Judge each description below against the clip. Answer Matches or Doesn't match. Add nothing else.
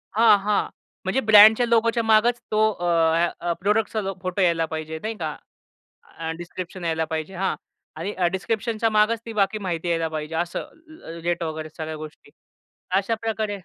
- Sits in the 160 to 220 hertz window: Matches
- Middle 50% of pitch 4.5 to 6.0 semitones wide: Matches